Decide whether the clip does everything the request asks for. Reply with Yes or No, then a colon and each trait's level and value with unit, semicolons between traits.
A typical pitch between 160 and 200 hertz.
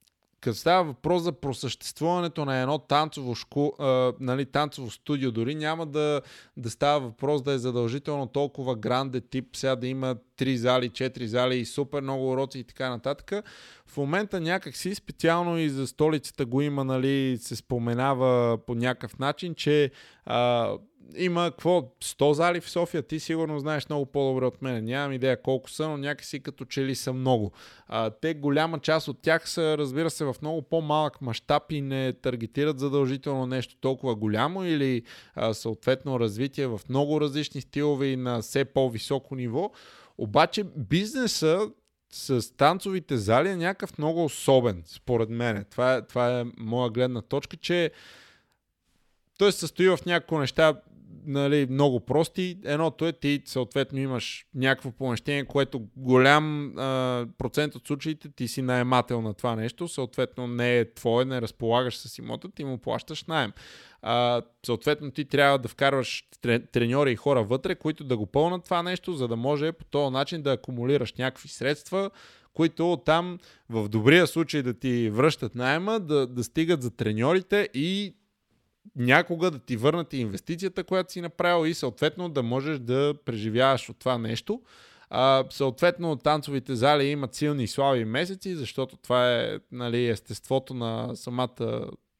No: low, 135 Hz